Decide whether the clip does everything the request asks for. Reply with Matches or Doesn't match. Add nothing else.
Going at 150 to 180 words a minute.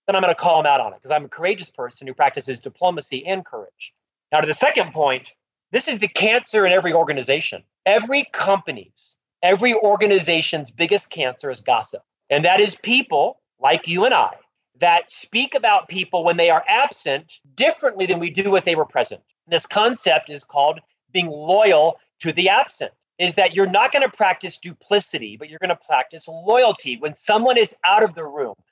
Doesn't match